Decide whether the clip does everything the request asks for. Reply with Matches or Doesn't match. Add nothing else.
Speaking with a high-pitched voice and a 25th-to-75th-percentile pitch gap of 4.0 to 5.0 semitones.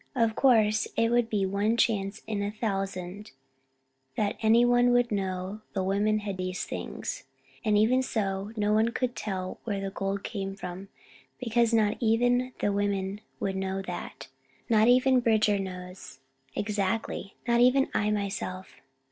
Doesn't match